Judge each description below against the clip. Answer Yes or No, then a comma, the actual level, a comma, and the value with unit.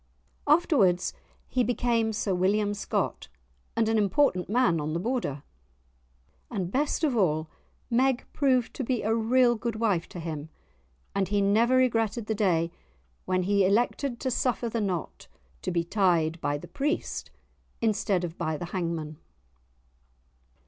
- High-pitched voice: Yes, high, 205 Hz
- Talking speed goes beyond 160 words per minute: No, average, 150 wpm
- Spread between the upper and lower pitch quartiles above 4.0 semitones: Yes, wide, 5.4 semitones